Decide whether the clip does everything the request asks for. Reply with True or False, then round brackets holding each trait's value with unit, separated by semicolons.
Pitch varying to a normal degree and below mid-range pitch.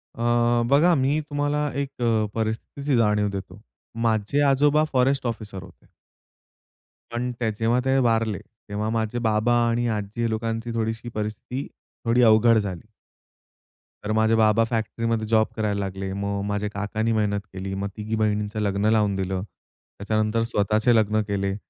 False (2.2 semitones; 110 Hz)